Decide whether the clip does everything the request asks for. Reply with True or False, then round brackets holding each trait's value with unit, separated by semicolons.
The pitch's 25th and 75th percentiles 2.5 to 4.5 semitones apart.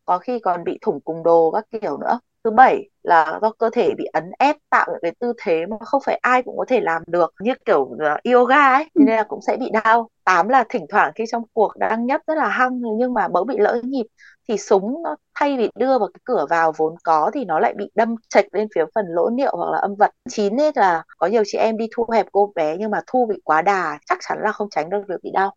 False (5.0 semitones)